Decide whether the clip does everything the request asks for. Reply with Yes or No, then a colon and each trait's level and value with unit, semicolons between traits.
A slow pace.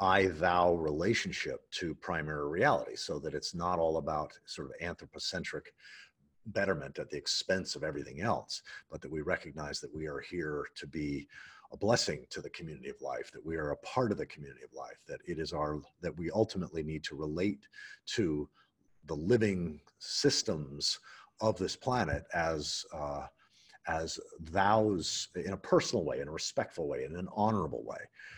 No: average, 175 wpm